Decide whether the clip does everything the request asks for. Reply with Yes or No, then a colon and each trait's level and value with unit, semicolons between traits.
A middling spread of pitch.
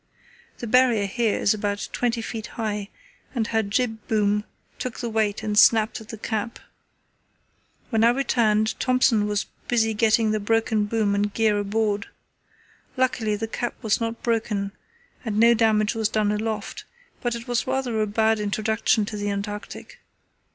No: narrow, 1.8 semitones